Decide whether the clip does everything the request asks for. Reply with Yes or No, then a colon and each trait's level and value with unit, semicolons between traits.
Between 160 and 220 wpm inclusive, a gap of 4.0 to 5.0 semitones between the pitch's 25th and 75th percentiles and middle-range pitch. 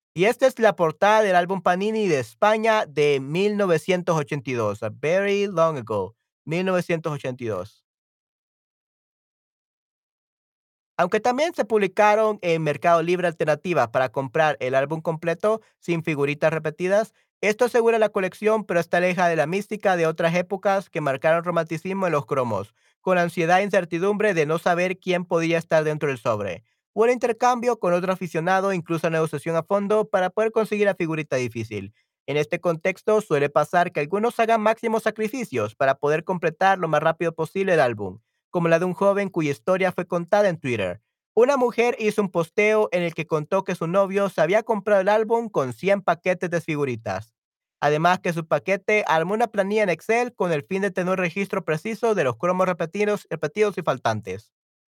Yes: average, 170 wpm; average, 4.5 semitones; medium, 180 Hz